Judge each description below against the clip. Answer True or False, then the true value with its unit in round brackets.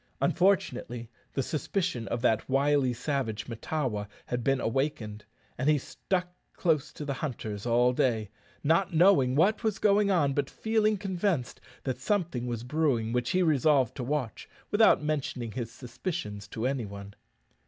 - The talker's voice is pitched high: False (135 Hz)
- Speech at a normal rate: True (155 wpm)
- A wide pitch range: True (5.9 semitones)